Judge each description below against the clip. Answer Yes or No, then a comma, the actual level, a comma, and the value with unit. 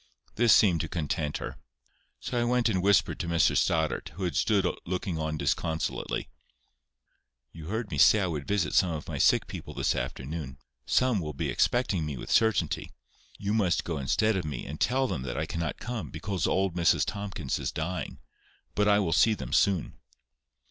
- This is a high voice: No, very low, 90 Hz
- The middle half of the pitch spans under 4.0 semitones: No, average, 4.9 semitones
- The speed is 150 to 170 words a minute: No, average, 190 wpm